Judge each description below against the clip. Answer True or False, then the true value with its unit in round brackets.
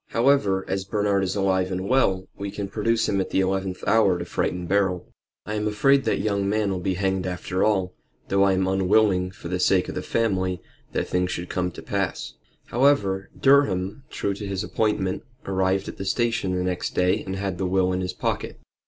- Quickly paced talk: True (210 wpm)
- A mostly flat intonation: True (1.8 semitones)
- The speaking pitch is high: False (95 Hz)